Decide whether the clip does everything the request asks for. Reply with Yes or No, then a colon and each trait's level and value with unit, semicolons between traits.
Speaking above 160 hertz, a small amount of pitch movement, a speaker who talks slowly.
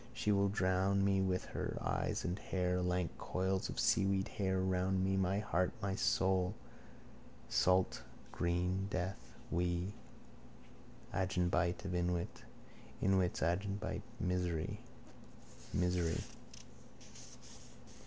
No: very low, 95 Hz; narrow, 1.3 semitones; slow, 105 wpm